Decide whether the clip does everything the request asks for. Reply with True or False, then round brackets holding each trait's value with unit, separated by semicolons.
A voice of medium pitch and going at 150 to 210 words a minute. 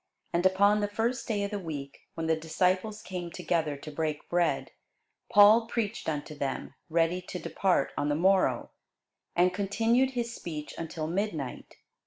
True (180 Hz; 160 wpm)